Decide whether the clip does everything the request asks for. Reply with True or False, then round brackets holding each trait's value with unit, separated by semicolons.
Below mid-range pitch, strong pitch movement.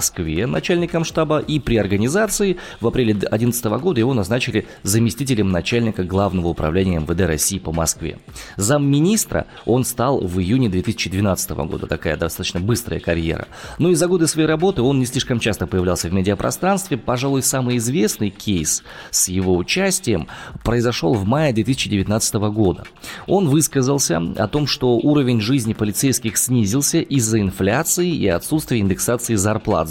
True (115 Hz; 6.3 semitones)